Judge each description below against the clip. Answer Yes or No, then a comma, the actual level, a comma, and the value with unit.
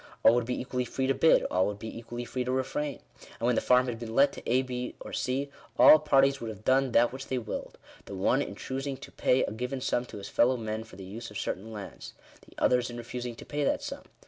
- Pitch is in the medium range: No, low, 125 Hz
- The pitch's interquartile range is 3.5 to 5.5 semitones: No, narrow, 2.4 semitones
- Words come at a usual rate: No, fast, 275 wpm